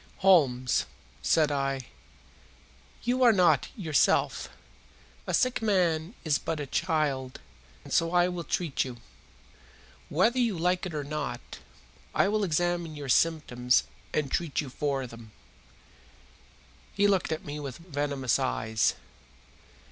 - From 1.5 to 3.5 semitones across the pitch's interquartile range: No, average, 4.6 semitones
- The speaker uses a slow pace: Yes, slow, 130 wpm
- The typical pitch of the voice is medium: Yes, medium, 155 Hz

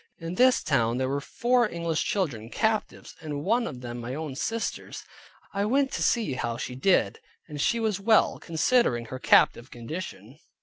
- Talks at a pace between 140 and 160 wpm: No, average, 175 wpm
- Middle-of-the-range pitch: Yes, medium, 160 Hz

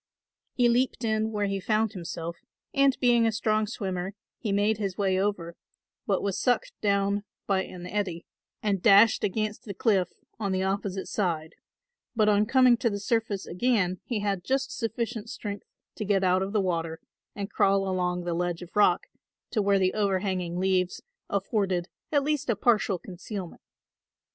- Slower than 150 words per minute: No, average, 170 wpm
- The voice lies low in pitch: No, high, 200 Hz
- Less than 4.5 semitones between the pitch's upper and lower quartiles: Yes, average, 2.9 semitones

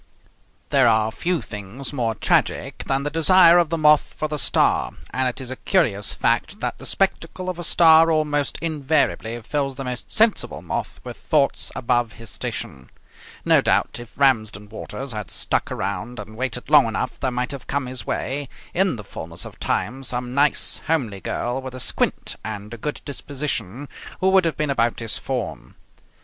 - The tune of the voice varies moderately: Yes, average, 4.9 semitones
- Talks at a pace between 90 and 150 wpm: No, average, 185 wpm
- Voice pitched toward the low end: Yes, low, 130 Hz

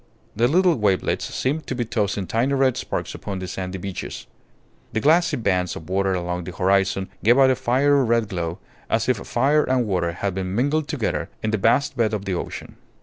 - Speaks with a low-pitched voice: Yes, low, 110 Hz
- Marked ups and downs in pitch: Yes, wide, 5.7 semitones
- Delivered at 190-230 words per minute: Yes, fast, 205 wpm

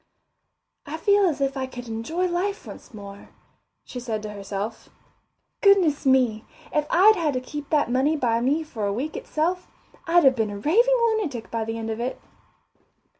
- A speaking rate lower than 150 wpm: No, average, 180 wpm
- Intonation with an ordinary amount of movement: No, wide, 6.8 semitones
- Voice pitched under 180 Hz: No, very high, 270 Hz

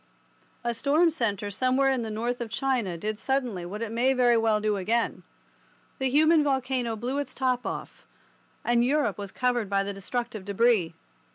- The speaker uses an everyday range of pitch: Yes, average, 3.7 semitones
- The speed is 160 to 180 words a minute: Yes, average, 175 wpm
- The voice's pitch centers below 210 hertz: No, high, 235 Hz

